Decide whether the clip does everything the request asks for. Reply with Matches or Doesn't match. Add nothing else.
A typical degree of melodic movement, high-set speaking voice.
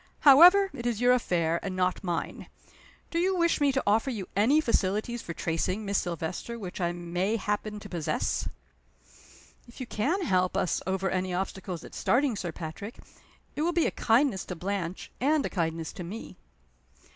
Doesn't match